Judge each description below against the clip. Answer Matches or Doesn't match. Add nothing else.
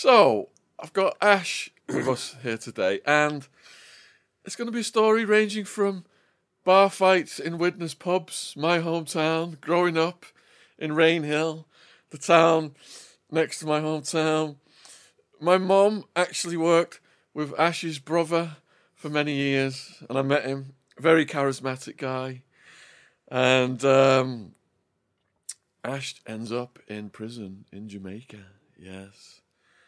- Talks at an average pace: Doesn't match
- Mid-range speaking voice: Matches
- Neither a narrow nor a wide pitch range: Matches